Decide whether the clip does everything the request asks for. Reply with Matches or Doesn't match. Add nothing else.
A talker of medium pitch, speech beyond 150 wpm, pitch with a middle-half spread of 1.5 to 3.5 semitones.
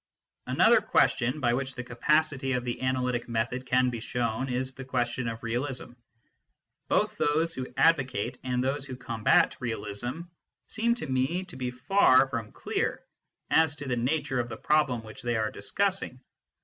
Doesn't match